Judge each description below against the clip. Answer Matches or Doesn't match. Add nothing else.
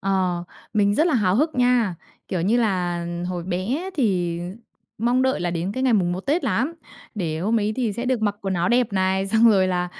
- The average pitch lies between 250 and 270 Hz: Doesn't match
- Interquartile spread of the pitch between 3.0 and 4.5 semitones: Doesn't match